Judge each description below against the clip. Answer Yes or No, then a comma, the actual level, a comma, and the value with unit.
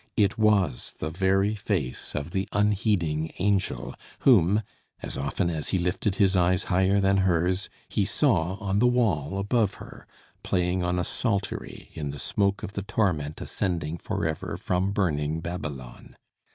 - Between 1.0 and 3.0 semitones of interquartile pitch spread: No, average, 3.7 semitones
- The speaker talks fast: No, average, 155 wpm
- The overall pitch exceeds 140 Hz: No, very low, 95 Hz